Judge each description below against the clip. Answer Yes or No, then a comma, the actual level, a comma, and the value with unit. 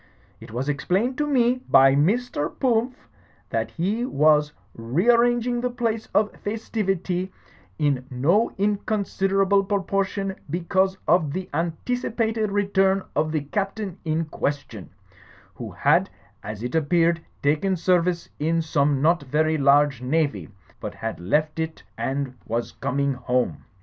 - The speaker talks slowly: Yes, slow, 130 wpm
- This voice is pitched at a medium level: Yes, medium, 170 Hz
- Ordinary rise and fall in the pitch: No, wide, 6.1 semitones